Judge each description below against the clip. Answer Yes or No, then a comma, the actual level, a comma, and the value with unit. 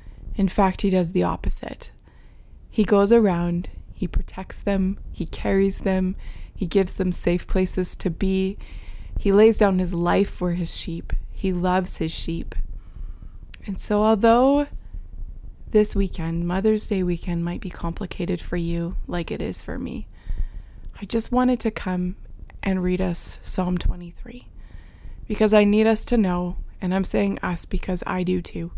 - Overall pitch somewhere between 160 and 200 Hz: Yes, medium, 185 Hz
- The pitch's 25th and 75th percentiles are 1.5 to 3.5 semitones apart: Yes, average, 2.9 semitones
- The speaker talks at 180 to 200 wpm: No, average, 160 wpm